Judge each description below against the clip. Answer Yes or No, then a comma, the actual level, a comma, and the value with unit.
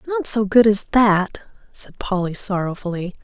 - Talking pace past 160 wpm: No, average, 150 wpm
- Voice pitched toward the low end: No, high, 205 Hz